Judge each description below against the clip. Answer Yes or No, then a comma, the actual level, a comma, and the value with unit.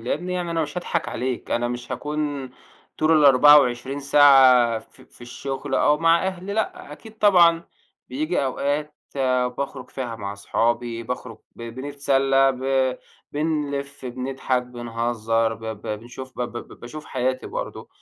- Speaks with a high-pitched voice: No, low, 135 Hz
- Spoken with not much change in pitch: No, average, 3.6 semitones